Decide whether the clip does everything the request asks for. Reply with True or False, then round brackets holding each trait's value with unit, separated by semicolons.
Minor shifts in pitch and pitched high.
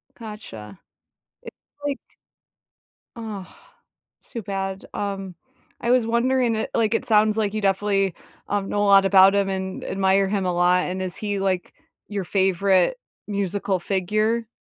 True (2.1 semitones; 195 Hz)